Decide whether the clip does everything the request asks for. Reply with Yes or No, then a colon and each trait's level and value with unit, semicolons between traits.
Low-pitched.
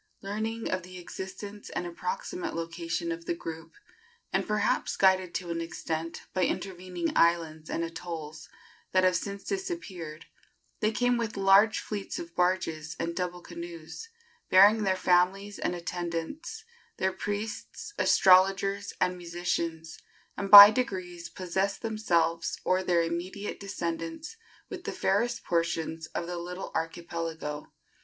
No: medium, 180 Hz